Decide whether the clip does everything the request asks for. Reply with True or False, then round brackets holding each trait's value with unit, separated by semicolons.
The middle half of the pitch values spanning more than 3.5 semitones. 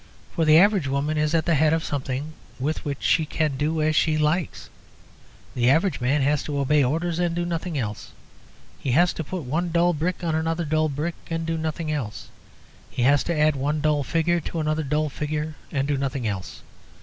False (2.5 semitones)